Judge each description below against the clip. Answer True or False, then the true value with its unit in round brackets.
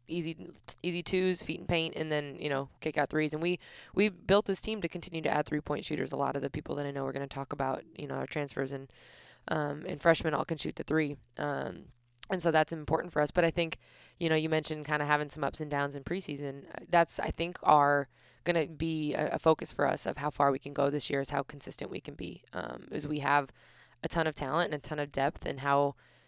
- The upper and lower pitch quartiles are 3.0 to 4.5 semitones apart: False (2.6 semitones)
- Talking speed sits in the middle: False (260 wpm)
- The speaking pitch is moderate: True (150 Hz)